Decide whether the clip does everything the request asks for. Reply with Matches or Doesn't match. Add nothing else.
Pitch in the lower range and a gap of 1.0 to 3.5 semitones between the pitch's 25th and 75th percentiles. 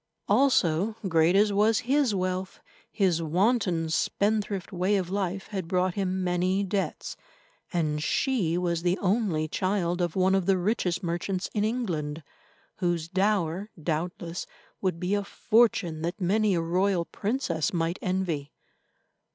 Doesn't match